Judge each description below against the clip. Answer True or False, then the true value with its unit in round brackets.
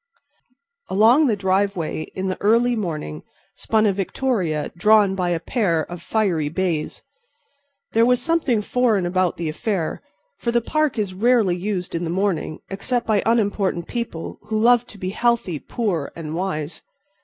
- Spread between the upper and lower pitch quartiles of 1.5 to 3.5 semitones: False (4.8 semitones)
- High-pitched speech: True (195 Hz)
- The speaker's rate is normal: True (155 wpm)